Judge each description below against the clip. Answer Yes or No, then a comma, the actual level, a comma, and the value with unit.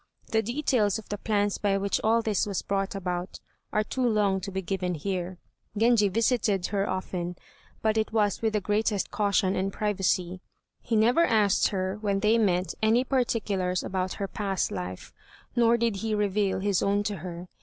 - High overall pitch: Yes, high, 205 Hz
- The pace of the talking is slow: No, average, 180 wpm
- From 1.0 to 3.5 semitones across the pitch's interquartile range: Yes, narrow, 2.6 semitones